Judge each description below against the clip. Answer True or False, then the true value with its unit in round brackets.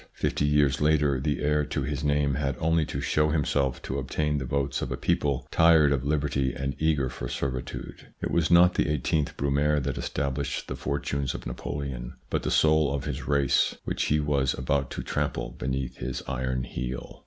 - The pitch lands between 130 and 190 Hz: False (70 Hz)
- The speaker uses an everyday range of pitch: False (2.0 semitones)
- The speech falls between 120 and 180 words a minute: False (190 wpm)